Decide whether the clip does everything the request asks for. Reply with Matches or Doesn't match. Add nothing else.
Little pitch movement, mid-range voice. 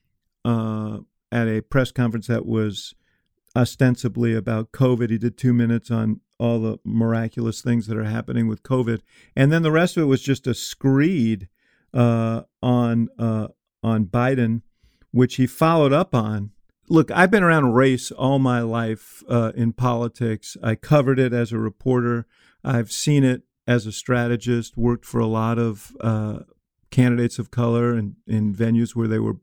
Doesn't match